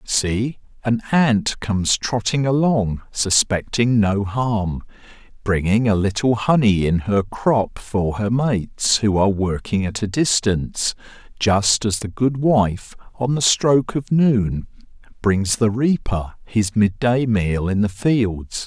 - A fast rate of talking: No, average, 140 wpm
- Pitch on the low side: Yes, low, 110 Hz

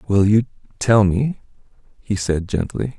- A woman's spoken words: No, male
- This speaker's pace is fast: No, average, 140 wpm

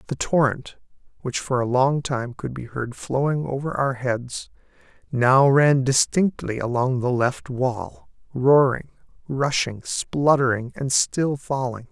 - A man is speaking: Yes, male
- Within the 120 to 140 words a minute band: Yes, slow, 135 wpm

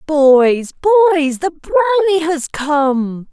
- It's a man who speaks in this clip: No, female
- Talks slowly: Yes, slow, 110 wpm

